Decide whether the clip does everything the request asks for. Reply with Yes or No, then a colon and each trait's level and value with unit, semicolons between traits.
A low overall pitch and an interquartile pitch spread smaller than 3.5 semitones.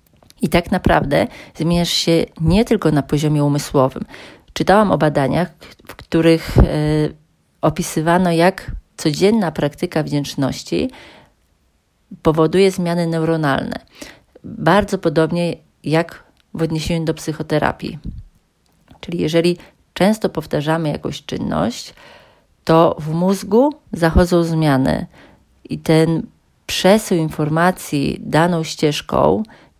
No: medium, 165 Hz; narrow, 2.5 semitones